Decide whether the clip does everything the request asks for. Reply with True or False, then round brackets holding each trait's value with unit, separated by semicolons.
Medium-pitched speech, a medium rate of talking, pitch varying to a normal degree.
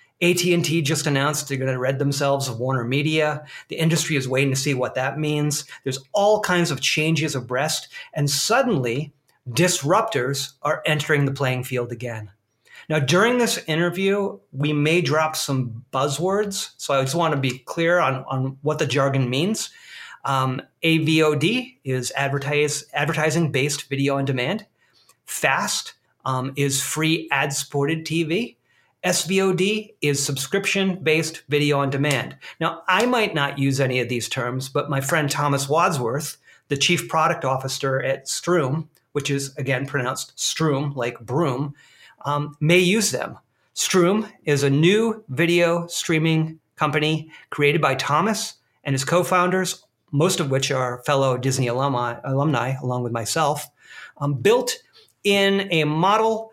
True (145 Hz; 145 wpm; 3.9 semitones)